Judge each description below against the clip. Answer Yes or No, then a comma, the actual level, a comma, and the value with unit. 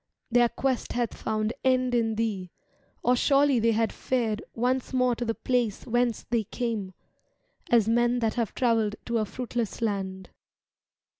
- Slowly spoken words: No, average, 155 wpm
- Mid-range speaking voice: No, high, 235 Hz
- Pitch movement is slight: Yes, narrow, 2.1 semitones